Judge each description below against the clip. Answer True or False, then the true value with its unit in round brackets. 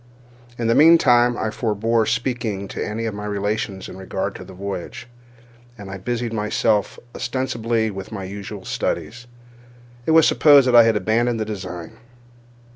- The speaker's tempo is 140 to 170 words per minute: True (165 wpm)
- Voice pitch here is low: True (110 Hz)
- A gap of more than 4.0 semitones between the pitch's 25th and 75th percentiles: False (3.1 semitones)